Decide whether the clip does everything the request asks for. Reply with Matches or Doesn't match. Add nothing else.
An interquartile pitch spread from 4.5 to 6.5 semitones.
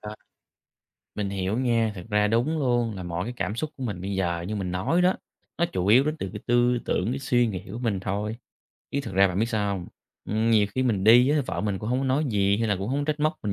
Doesn't match